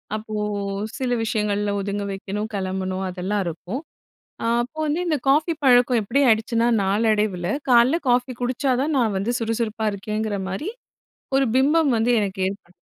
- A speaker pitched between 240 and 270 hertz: No, high, 220 Hz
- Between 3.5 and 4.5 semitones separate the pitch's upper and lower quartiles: Yes, average, 4.0 semitones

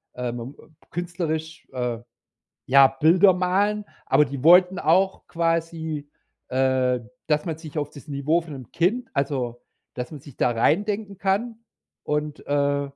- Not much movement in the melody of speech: No, average, 4.5 semitones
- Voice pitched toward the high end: No, medium, 155 Hz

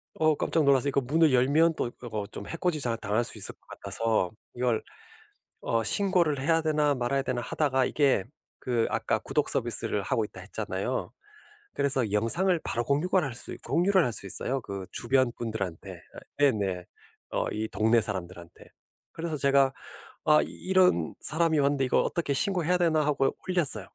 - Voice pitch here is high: No, low, 135 Hz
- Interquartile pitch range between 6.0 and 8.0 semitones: No, wide, 5.4 semitones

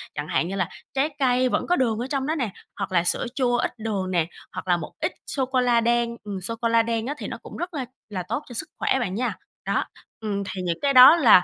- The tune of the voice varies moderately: Yes, average, 4.8 semitones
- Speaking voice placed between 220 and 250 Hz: Yes, high, 235 Hz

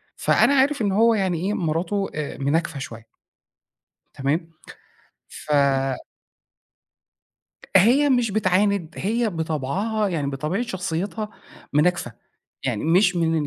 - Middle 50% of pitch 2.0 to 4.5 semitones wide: No, average, 5.1 semitones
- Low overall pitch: No, medium, 180 Hz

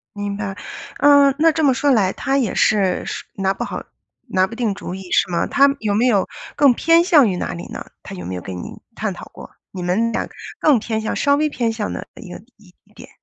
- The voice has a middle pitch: No, high, 220 Hz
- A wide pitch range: Yes, wide, 6.4 semitones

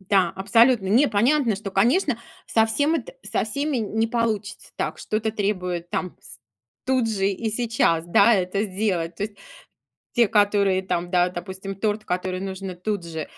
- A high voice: Yes, high, 205 Hz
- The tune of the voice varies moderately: Yes, average, 3.3 semitones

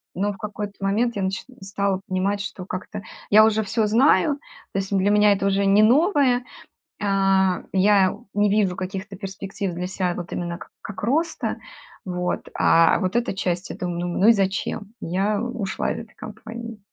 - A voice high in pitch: Yes, high, 200 Hz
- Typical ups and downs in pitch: No, narrow, 2.3 semitones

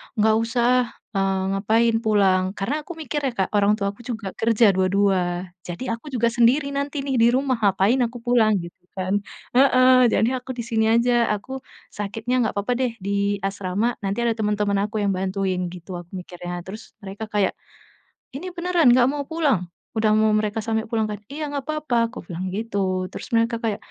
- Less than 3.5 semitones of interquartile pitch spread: No, average, 4.0 semitones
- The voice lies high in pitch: Yes, high, 220 Hz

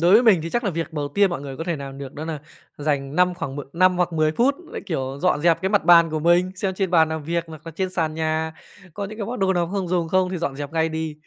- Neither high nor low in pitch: Yes, medium, 165 Hz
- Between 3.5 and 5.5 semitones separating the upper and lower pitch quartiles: No, average, 2.9 semitones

